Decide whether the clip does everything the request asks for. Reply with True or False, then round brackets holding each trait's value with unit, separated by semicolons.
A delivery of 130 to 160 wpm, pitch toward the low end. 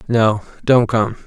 True (140 wpm; 115 Hz)